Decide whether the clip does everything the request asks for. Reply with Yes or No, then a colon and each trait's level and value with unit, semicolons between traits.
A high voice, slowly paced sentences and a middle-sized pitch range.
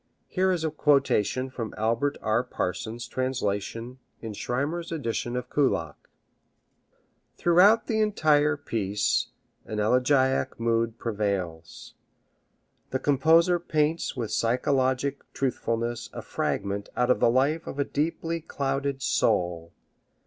No: low, 130 Hz; slow, 115 wpm; average, 4.6 semitones